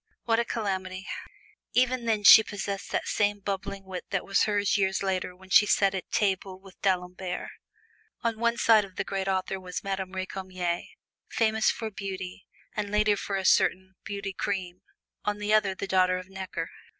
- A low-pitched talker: No, high, 195 Hz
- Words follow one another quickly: No, average, 175 wpm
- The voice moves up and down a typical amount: No, narrow, 1.7 semitones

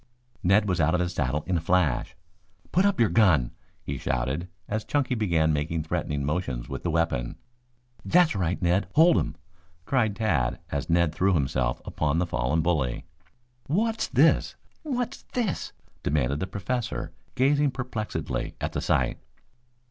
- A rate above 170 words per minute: No, average, 155 wpm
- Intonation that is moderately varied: No, wide, 7.0 semitones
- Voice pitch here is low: Yes, very low, 90 Hz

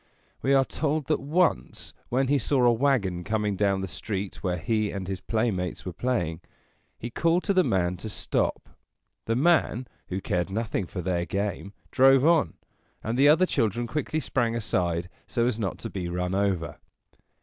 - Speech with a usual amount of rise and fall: No, wide, 6.2 semitones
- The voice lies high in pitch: No, low, 110 Hz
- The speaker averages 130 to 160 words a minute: No, average, 180 wpm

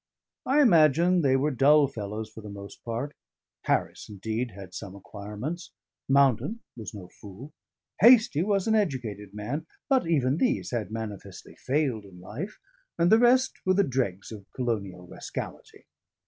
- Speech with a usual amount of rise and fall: No, wide, 8.2 semitones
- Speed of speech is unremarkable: Yes, average, 150 wpm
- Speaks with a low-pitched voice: Yes, low, 130 Hz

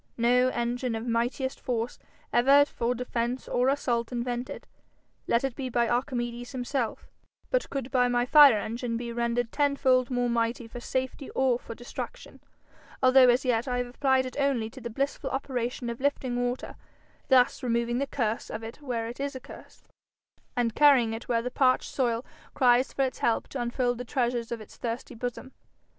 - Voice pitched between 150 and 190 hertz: No, high, 245 Hz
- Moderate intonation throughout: No, narrow, 1.8 semitones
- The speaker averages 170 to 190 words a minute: Yes, average, 180 wpm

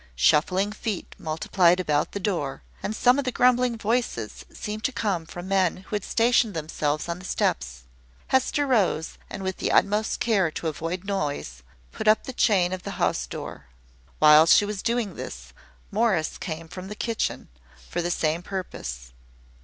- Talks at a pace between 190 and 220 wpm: No, average, 170 wpm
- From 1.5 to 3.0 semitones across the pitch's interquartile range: No, average, 5.3 semitones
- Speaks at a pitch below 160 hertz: No, medium, 185 Hz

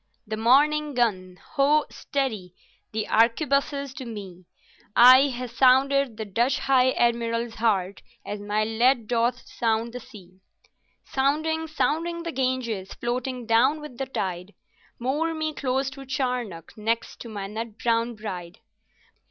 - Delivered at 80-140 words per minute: Yes, slow, 135 wpm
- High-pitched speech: Yes, high, 240 Hz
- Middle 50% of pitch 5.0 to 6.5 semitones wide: No, average, 3.9 semitones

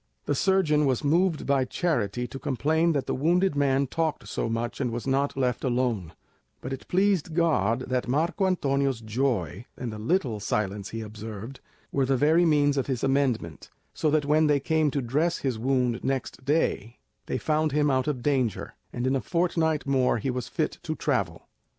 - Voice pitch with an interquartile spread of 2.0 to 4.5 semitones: Yes, average, 4.0 semitones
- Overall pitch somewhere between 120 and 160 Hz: Yes, low, 135 Hz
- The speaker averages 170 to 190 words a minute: Yes, average, 185 wpm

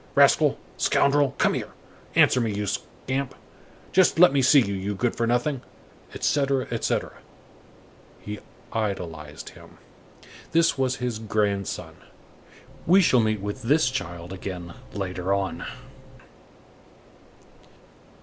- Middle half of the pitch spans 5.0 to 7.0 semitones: Yes, average, 5.3 semitones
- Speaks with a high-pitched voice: No, low, 115 Hz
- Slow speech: Yes, slow, 110 wpm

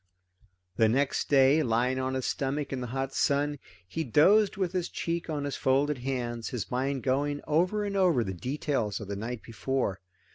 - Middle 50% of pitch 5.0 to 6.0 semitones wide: No, average, 3.2 semitones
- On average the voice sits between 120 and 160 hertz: Yes, low, 135 Hz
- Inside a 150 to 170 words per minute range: No, average, 185 wpm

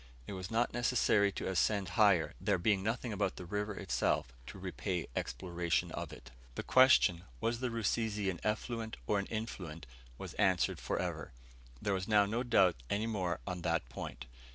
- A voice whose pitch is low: Yes, low, 100 Hz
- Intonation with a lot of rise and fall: No, average, 3.8 semitones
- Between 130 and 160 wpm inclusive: No, average, 175 wpm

